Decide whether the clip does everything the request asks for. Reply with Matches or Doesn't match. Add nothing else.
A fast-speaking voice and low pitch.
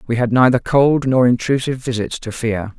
Doesn't match